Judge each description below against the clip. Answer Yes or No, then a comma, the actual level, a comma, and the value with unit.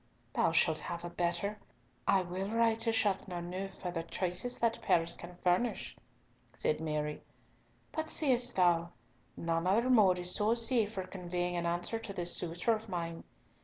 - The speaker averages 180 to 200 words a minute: No, average, 165 wpm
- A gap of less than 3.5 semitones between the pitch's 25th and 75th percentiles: No, average, 4.4 semitones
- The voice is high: No, medium, 180 Hz